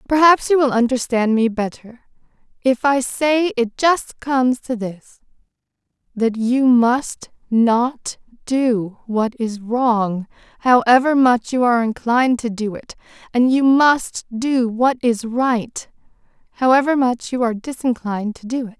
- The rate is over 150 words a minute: No, average, 145 wpm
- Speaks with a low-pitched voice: No, high, 245 Hz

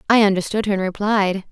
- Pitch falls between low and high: No, high, 200 Hz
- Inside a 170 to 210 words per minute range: Yes, average, 200 wpm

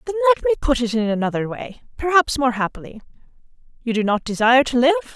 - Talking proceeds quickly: No, average, 185 wpm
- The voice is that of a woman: Yes, female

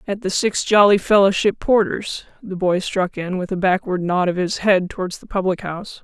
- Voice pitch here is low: No, high, 190 Hz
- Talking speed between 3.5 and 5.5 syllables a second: Yes, 5.0 syllables/s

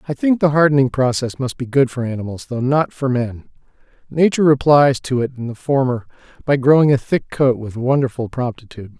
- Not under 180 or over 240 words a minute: Yes, average, 195 wpm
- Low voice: Yes, low, 130 Hz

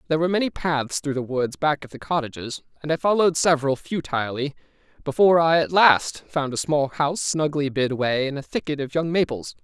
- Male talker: Yes, male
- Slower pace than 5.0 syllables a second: No, 6.0 syllables/s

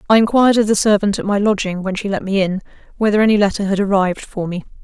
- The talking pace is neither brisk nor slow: No, fast, 250 wpm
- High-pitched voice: Yes, high, 200 Hz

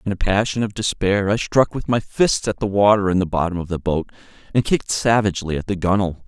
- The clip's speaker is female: No, male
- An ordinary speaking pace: No, fast, 240 wpm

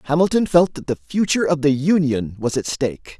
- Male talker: Yes, male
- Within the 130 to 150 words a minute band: No, fast, 205 wpm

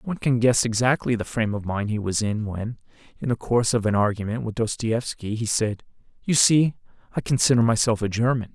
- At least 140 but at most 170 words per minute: No, fast, 205 wpm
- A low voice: Yes, low, 115 Hz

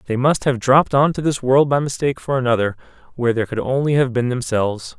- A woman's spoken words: No, male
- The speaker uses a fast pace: Yes, fast, 230 wpm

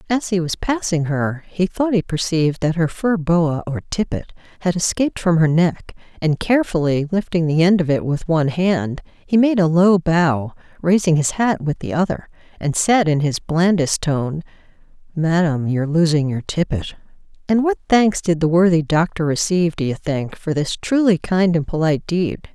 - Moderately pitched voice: Yes, medium, 170 Hz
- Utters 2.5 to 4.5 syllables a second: No, 4.9 syllables/s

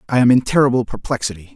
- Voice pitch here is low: Yes, low, 120 Hz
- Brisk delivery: No, average, 195 wpm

